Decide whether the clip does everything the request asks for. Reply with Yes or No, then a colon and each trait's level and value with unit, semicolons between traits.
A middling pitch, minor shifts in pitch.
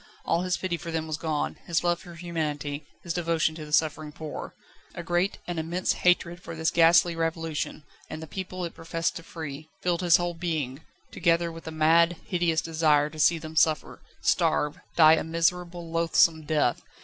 Yes: medium, 165 Hz; narrow, 1.6 semitones